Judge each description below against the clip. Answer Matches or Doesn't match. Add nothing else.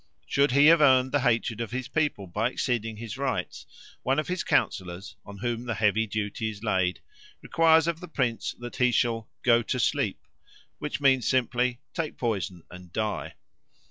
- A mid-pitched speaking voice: Doesn't match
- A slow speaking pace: Doesn't match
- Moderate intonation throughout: Matches